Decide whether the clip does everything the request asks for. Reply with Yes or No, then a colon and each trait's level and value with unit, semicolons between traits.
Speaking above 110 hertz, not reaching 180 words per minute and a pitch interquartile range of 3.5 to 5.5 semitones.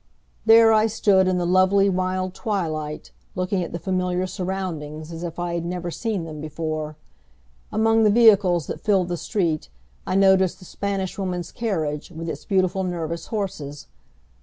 No: medium, 185 Hz; average, 160 wpm; average, 2.8 semitones